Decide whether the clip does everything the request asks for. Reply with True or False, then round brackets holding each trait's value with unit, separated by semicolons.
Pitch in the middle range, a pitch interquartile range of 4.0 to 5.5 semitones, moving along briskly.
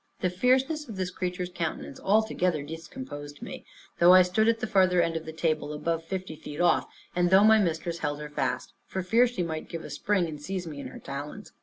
False (175 Hz; 3.5 semitones; 220 wpm)